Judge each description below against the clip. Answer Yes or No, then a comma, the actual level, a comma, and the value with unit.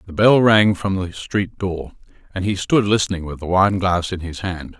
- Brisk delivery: Yes, fast, 225 wpm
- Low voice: Yes, very low, 95 Hz